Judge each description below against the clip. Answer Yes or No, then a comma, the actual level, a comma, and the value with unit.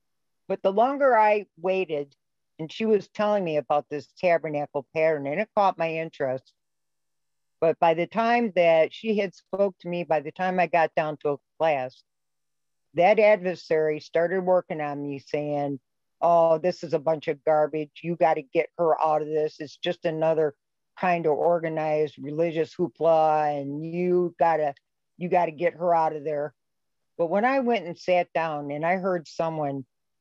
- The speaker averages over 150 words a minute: Yes, average, 175 wpm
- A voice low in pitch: No, medium, 165 Hz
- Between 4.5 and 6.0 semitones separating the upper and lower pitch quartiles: No, average, 2.8 semitones